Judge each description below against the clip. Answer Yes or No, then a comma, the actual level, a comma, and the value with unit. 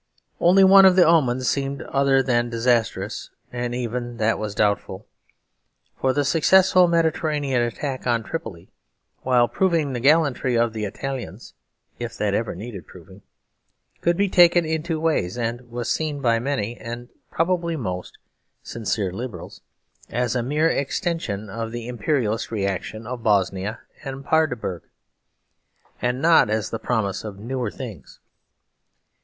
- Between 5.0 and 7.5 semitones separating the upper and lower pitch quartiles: Yes, average, 5.3 semitones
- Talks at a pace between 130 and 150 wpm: Yes, average, 140 wpm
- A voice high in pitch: No, low, 125 Hz